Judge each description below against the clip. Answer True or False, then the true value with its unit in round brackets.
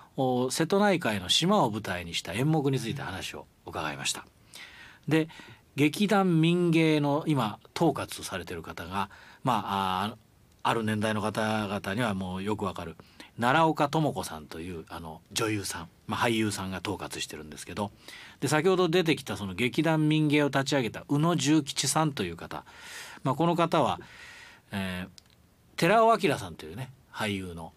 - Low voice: True (115 Hz)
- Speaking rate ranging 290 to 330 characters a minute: True (305 characters per minute)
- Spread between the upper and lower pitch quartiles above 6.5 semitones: True (8.1 semitones)